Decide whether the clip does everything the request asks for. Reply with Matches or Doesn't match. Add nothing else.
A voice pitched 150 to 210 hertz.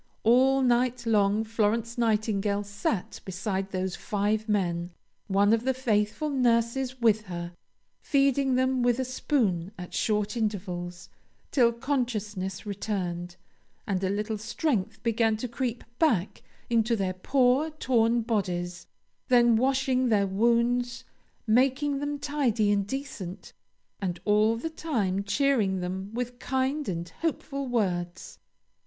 Doesn't match